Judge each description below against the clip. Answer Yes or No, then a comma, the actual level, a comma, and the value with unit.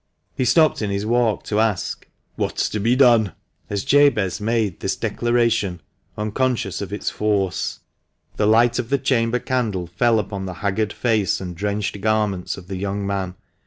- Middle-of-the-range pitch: No, low, 105 Hz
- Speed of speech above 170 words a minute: No, average, 165 wpm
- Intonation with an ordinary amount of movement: Yes, average, 3.2 semitones